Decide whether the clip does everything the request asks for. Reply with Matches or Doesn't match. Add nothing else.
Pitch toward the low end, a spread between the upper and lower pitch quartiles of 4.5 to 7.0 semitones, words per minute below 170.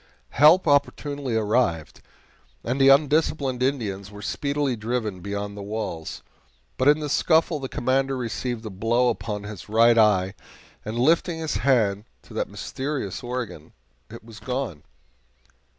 Matches